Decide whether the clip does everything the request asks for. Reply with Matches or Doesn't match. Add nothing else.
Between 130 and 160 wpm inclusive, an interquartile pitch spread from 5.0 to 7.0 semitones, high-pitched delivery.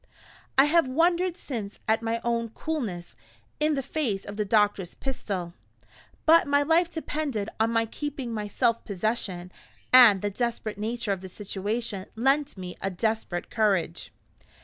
Matches